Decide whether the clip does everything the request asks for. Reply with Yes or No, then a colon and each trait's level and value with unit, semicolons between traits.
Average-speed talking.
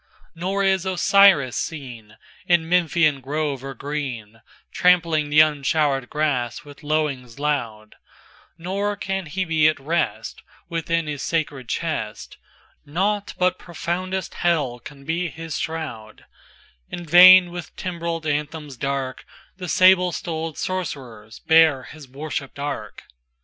No: slow, 105 wpm